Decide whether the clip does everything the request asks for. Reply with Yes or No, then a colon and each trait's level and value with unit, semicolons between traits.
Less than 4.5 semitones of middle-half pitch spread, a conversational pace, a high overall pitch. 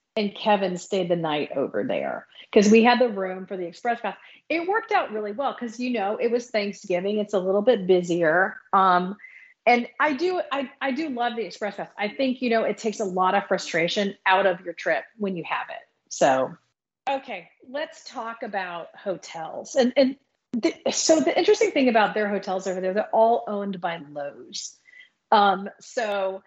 No: average, 4.9 semitones; average, 195 wpm; high, 210 Hz